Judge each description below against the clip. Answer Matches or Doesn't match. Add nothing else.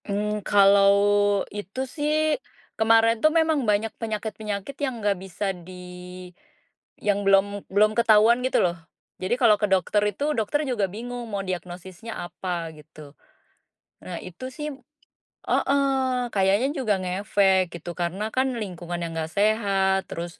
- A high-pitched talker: Matches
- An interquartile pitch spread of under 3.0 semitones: Doesn't match